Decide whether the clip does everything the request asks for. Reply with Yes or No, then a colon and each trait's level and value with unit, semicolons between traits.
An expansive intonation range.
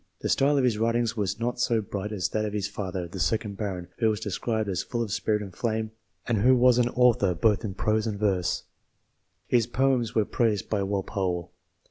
No: average, 3.0 semitones